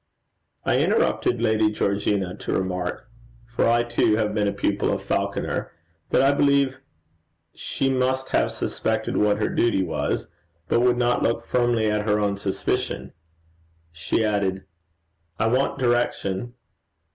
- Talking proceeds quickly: No, average, 140 wpm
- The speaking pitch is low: Yes, low, 110 Hz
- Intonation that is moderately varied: Yes, average, 3.3 semitones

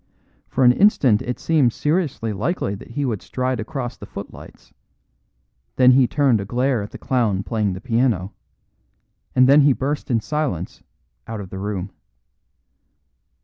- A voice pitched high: No, low, 125 Hz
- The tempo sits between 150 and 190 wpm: Yes, average, 155 wpm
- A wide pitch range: No, average, 4.6 semitones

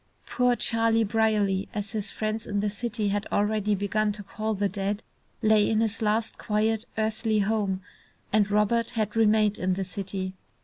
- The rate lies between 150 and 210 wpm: Yes, average, 170 wpm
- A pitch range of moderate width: No, narrow, 1.5 semitones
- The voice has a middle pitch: No, high, 210 Hz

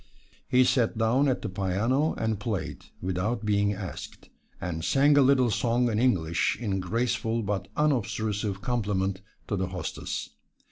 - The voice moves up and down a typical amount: Yes, average, 4.2 semitones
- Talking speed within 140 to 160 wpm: Yes, average, 145 wpm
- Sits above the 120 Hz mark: No, low, 110 Hz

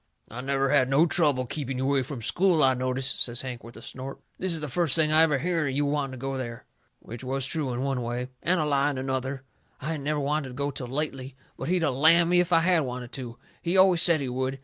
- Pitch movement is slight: No, average, 3.3 semitones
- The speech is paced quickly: Yes, fast, 265 wpm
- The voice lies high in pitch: No, low, 135 Hz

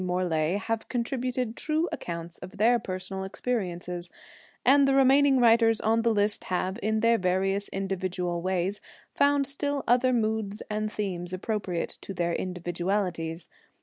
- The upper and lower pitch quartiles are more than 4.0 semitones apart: Yes, average, 4.5 semitones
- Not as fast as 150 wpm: Yes, average, 140 wpm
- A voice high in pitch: Yes, high, 205 Hz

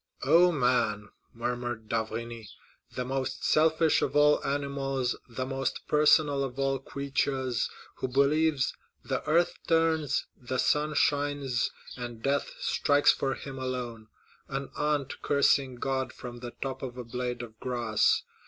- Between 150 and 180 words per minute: No, slow, 135 wpm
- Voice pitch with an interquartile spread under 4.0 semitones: Yes, average, 2.8 semitones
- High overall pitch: No, low, 135 Hz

